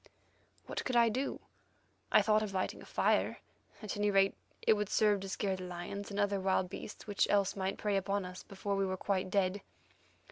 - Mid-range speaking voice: No, high, 200 Hz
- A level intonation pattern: Yes, narrow, 1.5 semitones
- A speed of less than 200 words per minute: No, fast, 205 wpm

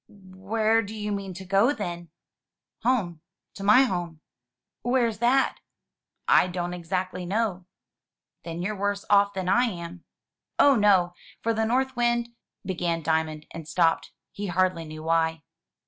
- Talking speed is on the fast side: No, average, 145 wpm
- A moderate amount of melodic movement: Yes, average, 4.2 semitones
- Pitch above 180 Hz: Yes, high, 190 Hz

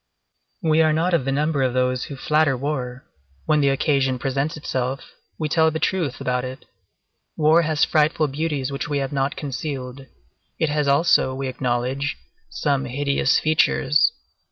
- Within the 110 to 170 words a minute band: Yes, average, 160 wpm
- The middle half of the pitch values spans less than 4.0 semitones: Yes, average, 2.7 semitones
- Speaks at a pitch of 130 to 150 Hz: Yes, medium, 140 Hz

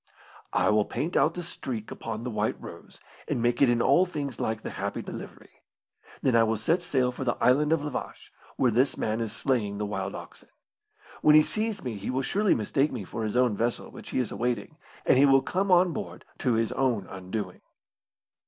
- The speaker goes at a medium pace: No, fast, 215 wpm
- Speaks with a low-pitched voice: Yes, low, 125 Hz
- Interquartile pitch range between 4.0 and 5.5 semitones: Yes, average, 4.6 semitones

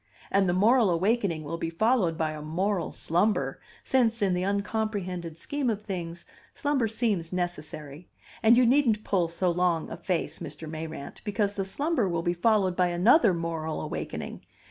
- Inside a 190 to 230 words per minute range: No, average, 165 wpm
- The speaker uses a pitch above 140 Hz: Yes, medium, 185 Hz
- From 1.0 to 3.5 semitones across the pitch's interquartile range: No, average, 4.6 semitones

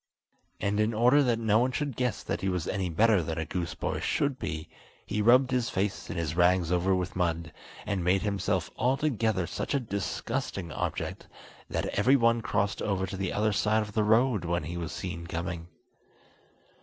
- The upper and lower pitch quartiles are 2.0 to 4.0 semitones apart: No, average, 4.9 semitones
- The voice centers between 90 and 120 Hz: Yes, low, 100 Hz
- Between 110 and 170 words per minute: No, average, 195 wpm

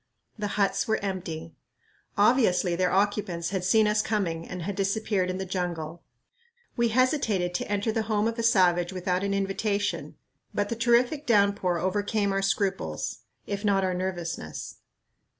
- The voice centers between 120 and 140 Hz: No, high, 195 Hz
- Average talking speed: Yes, average, 155 wpm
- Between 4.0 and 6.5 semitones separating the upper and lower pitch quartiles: No, average, 2.8 semitones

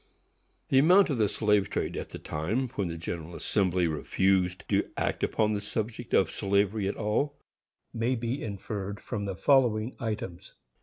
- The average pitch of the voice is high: No, low, 105 Hz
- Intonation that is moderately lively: Yes, average, 3.5 semitones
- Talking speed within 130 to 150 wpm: No, average, 165 wpm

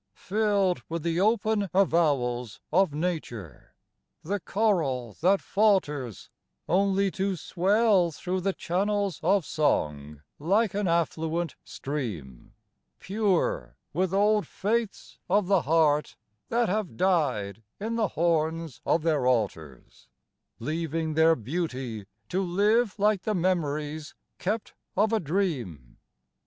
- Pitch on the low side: No, medium, 170 Hz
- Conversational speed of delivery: No, slow, 115 wpm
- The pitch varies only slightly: No, average, 5.3 semitones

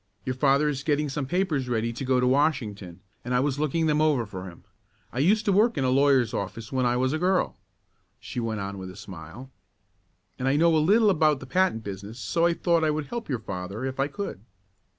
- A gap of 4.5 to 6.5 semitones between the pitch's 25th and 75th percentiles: Yes, average, 5.2 semitones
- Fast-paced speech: Yes, fast, 230 wpm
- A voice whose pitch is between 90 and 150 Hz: Yes, low, 135 Hz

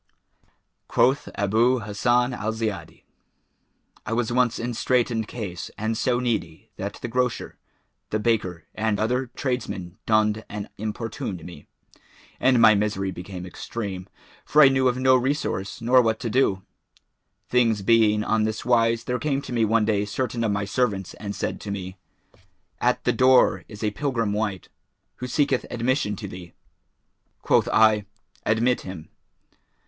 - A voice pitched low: Yes, low, 110 Hz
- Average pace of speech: Yes, average, 155 wpm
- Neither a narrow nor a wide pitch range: Yes, average, 3.3 semitones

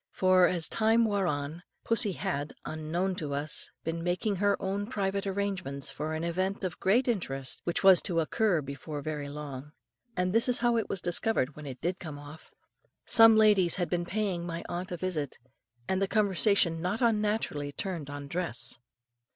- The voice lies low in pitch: No, medium, 180 Hz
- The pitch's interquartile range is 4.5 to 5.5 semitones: Yes, average, 4.9 semitones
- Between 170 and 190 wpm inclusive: Yes, average, 180 wpm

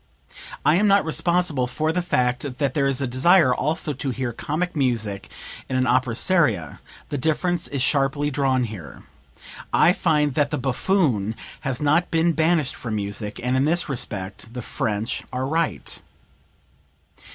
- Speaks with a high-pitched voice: No, low, 135 Hz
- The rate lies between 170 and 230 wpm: No, average, 160 wpm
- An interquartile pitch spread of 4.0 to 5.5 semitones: Yes, average, 4.4 semitones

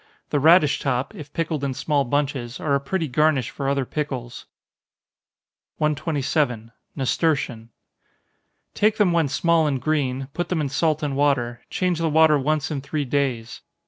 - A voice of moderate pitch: Yes, medium, 145 Hz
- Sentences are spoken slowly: No, average, 155 wpm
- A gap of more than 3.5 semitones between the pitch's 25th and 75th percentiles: No, average, 2.8 semitones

